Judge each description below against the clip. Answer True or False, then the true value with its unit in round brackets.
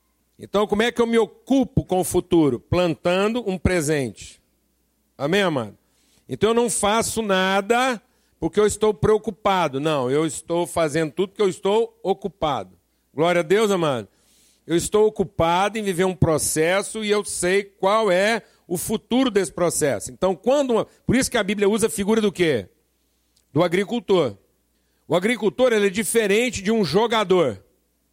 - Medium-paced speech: True (160 wpm)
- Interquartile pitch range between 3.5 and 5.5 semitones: True (4.8 semitones)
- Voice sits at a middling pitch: False (195 Hz)